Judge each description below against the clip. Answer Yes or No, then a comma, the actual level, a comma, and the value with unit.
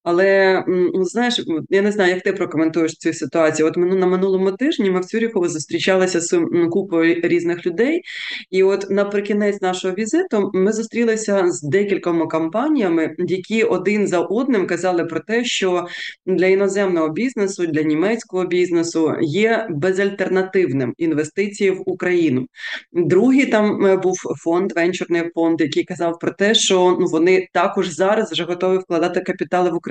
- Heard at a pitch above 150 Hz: Yes, medium, 185 Hz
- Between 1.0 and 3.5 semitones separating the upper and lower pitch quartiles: Yes, average, 2.8 semitones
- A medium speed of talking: Yes, average, 145 wpm